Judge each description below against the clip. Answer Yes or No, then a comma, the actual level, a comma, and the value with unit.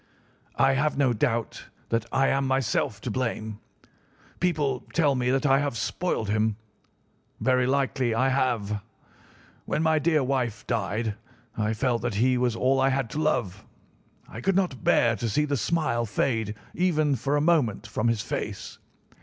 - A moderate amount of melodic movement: Yes, average, 3.7 semitones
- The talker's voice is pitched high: No, low, 130 Hz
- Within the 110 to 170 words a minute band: Yes, average, 165 wpm